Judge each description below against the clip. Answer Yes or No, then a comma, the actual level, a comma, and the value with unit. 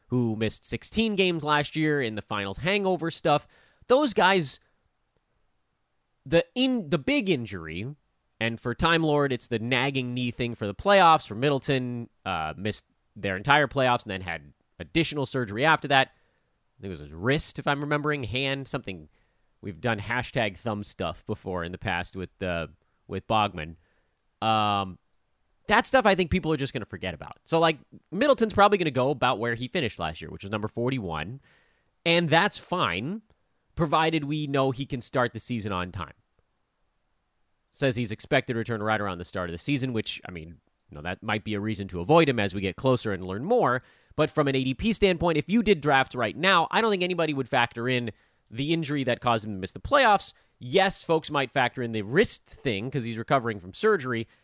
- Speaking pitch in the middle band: No, low, 125 Hz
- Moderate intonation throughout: No, wide, 6.6 semitones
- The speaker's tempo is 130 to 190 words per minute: No, average, 200 wpm